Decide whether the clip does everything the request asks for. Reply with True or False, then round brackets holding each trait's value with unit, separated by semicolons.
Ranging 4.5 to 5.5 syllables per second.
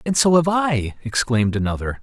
True (5.4 syllables/s)